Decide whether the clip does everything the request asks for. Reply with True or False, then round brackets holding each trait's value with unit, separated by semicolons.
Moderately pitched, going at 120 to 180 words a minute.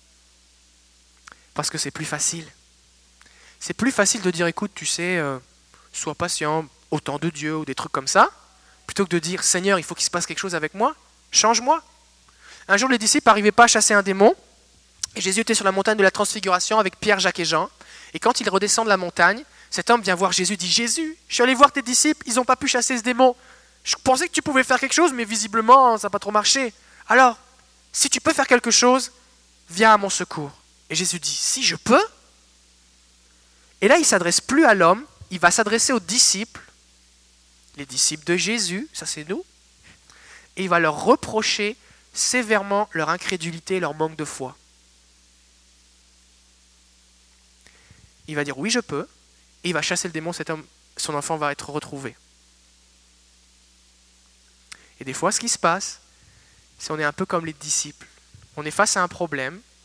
False (175 Hz; 195 wpm)